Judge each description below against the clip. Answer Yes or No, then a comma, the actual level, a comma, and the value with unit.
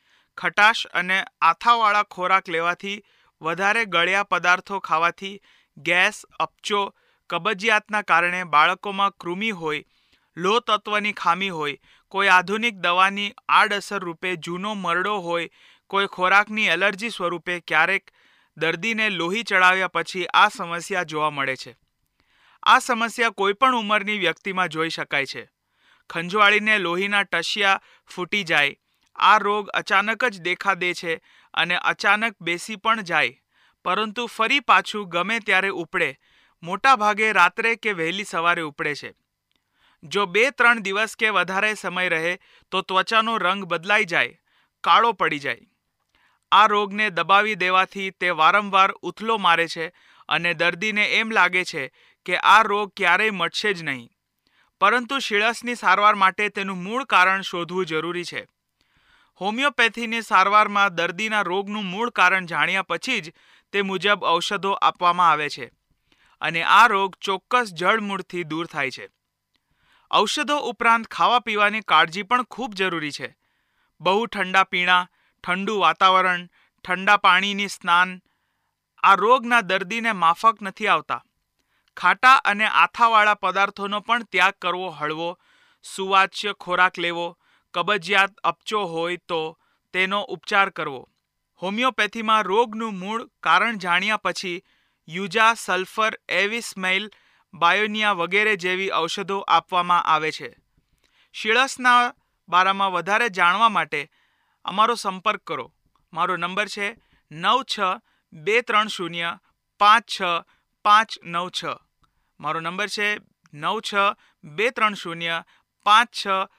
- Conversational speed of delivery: Yes, average, 120 wpm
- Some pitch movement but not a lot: Yes, average, 3.4 semitones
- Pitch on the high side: Yes, high, 195 Hz